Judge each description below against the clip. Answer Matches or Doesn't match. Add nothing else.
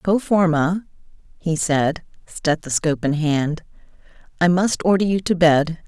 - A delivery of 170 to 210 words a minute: Doesn't match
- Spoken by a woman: Matches